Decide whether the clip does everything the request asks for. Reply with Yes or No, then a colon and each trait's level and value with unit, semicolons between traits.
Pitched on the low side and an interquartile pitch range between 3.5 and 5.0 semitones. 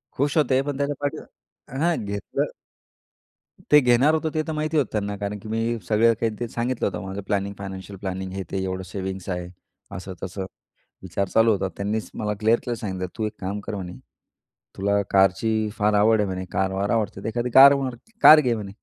Yes: low, 105 Hz; average, 3.9 semitones